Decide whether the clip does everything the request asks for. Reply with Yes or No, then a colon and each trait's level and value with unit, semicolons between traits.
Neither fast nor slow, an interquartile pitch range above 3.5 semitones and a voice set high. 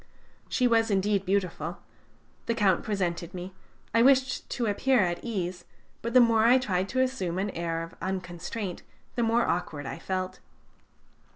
Yes: average, 160 wpm; average, 4.6 semitones; high, 195 Hz